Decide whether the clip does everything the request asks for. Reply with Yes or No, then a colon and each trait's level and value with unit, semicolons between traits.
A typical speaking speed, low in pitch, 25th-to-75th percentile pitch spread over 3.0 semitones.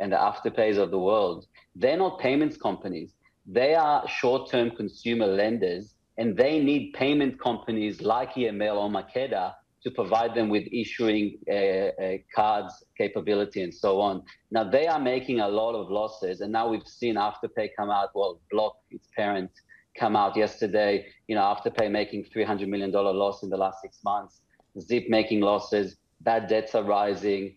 No: average, 165 wpm; low, 110 Hz; narrow, 2.5 semitones